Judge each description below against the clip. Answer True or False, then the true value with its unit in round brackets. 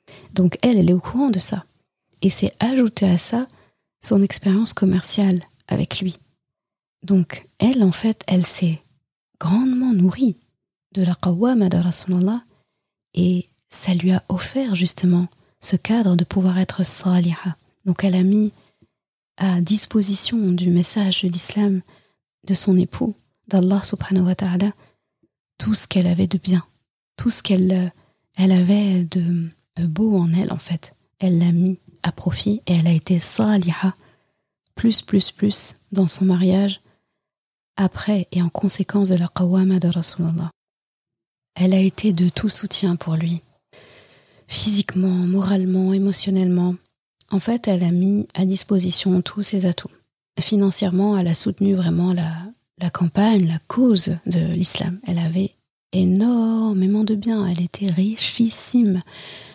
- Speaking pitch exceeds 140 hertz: True (185 Hz)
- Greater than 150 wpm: False (145 wpm)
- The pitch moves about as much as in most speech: False (2.3 semitones)